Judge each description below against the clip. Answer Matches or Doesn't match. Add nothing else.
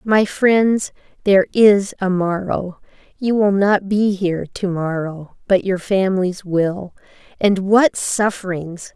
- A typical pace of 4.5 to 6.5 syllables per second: Doesn't match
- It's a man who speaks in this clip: Doesn't match